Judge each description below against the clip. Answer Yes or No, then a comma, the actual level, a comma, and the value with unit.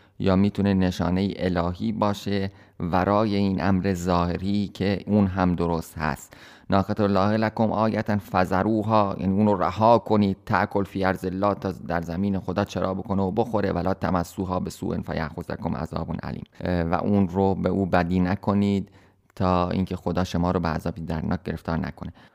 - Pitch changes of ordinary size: No, narrow, 1.9 semitones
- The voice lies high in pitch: No, very low, 95 Hz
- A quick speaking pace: Yes, fast, 165 wpm